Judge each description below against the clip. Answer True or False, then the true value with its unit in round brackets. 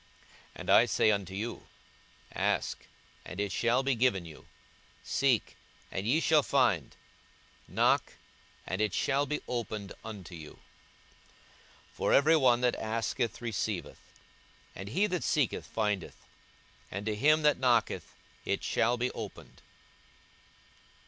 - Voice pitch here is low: True (115 Hz)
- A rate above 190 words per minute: False (135 wpm)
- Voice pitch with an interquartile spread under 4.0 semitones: False (4.7 semitones)